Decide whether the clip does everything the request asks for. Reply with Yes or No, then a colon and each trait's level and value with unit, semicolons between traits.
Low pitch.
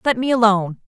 No: high, 225 Hz